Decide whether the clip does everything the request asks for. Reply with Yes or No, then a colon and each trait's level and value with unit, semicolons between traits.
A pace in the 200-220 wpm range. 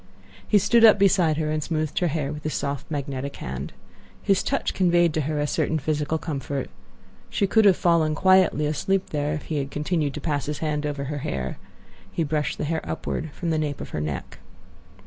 Yes: fast, 205 wpm